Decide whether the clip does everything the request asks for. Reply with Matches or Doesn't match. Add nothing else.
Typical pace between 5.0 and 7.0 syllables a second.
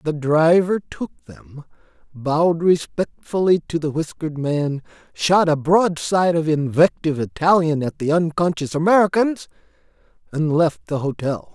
Doesn't match